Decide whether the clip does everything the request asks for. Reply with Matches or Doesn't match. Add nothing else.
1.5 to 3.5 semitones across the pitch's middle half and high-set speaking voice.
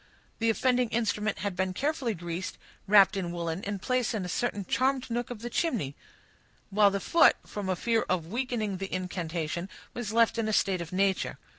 Doesn't match